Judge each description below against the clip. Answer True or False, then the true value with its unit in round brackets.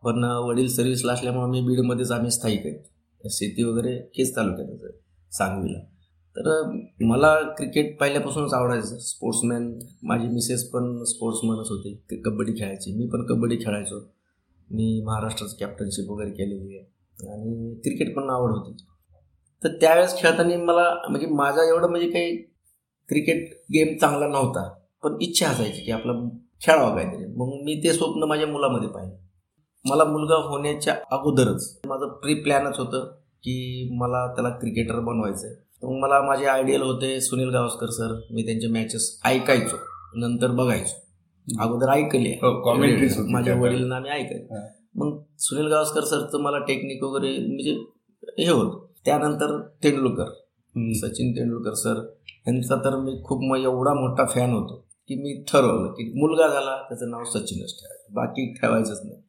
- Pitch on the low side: True (125 Hz)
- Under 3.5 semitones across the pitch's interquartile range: False (4.0 semitones)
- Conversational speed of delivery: False (145 wpm)